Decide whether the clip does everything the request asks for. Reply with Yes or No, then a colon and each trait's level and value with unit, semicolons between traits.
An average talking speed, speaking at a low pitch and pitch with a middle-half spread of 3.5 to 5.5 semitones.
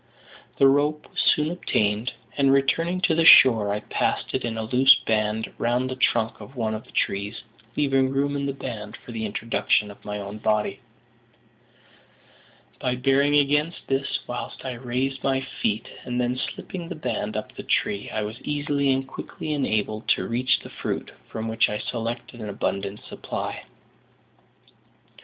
Yes: average, 170 wpm; low, 125 Hz; average, 4.2 semitones